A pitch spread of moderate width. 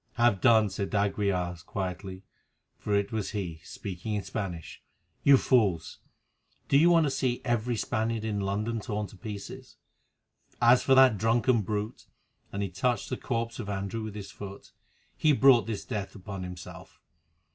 Yes: average, 3.2 semitones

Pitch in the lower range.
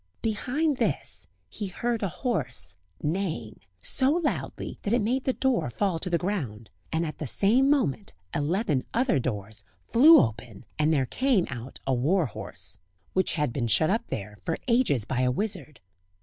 No: medium, 170 Hz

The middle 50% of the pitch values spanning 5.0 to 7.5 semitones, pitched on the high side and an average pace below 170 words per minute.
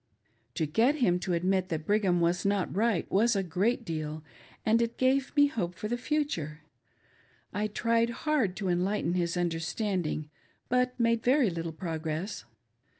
Yes: wide, 5.5 semitones; high, 195 Hz; average, 155 wpm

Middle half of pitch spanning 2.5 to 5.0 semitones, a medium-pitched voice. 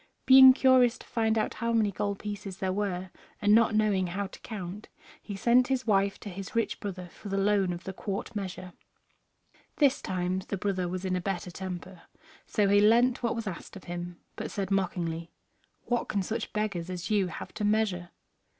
No: average, 3.0 semitones; high, 200 Hz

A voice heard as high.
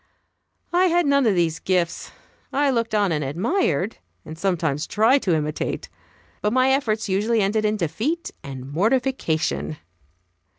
Yes: high, 205 Hz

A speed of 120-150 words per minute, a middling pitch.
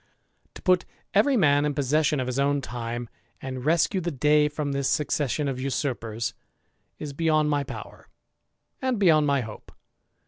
Yes: average, 145 wpm; medium, 145 Hz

